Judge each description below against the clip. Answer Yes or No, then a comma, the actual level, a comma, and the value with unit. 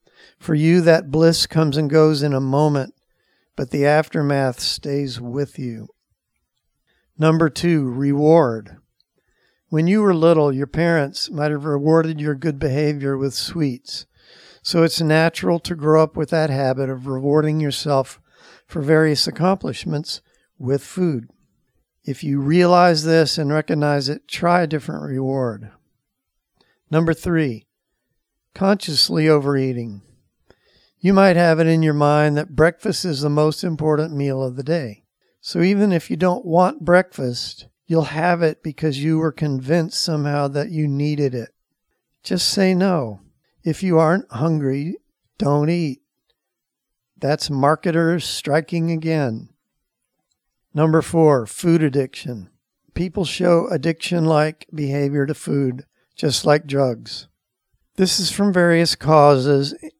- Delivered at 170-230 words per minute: No, slow, 135 wpm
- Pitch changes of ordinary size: Yes, average, 3.0 semitones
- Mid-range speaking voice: Yes, medium, 155 Hz